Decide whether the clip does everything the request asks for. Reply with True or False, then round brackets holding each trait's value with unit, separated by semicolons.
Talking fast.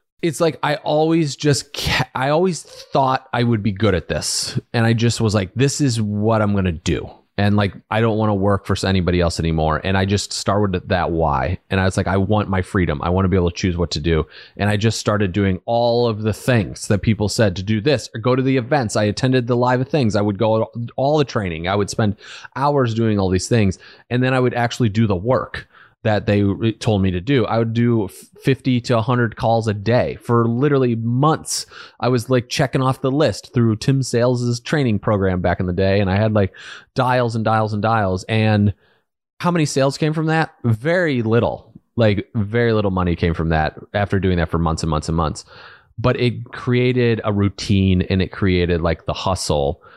True (225 wpm)